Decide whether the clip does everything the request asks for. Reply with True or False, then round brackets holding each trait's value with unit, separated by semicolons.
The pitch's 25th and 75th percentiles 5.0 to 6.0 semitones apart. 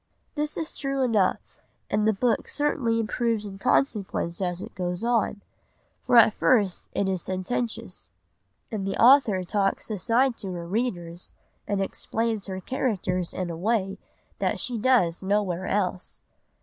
False (4.0 semitones)